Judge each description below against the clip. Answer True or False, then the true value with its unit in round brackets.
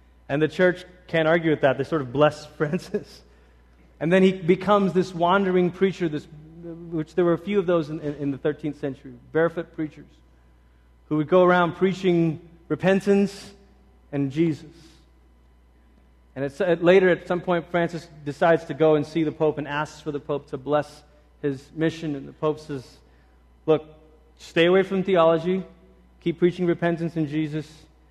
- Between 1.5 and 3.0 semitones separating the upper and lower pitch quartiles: False (3.6 semitones)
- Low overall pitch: False (155 Hz)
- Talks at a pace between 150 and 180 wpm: True (175 wpm)